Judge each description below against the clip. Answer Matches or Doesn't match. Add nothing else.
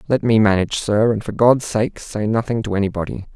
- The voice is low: Matches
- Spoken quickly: Matches